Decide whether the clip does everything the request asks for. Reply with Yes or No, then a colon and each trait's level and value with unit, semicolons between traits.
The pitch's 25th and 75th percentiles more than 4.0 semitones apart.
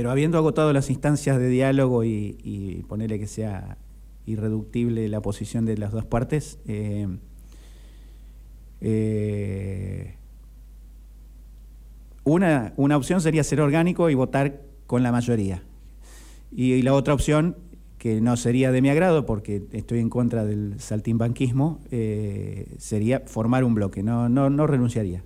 Yes: average, 5.0 semitones